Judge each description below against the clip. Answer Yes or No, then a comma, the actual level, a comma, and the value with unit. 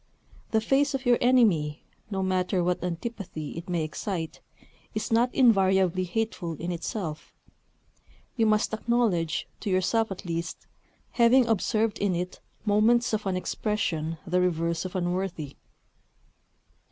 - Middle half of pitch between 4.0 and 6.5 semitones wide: Yes, average, 4.5 semitones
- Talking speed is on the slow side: Yes, slow, 130 wpm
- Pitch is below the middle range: No, high, 190 Hz